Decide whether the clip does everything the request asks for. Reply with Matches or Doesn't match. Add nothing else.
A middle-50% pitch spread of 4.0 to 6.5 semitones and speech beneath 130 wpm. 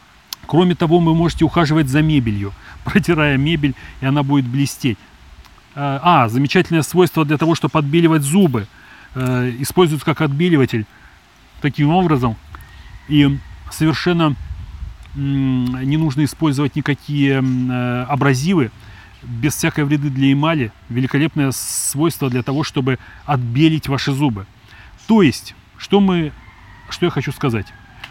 Matches